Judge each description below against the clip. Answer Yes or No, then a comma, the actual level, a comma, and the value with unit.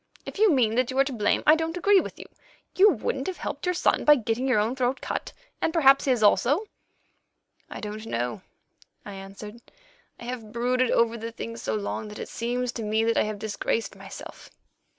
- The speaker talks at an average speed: No, fast, 210 wpm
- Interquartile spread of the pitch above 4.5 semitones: No, average, 3.9 semitones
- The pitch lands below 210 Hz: No, high, 235 Hz